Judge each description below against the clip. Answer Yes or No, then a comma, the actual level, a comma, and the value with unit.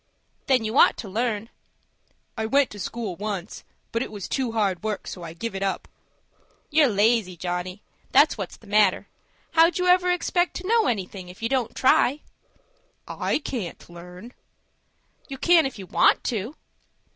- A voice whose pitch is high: Yes, high, 220 Hz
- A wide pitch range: Yes, wide, 5.8 semitones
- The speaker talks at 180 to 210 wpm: No, average, 165 wpm